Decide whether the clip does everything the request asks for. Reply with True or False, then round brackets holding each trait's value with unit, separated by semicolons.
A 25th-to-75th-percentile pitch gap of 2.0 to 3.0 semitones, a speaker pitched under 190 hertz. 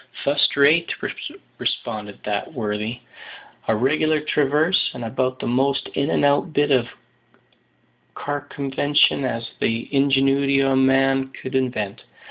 True (2.6 semitones; 135 Hz)